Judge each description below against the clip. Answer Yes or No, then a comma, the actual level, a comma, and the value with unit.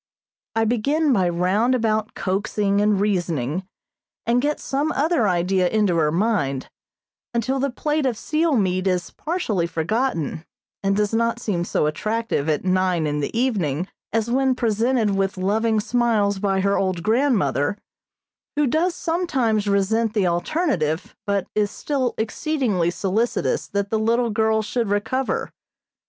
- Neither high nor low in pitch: No, high, 215 Hz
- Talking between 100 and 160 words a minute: Yes, average, 145 wpm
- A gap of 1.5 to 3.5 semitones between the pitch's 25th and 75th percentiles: No, average, 4.6 semitones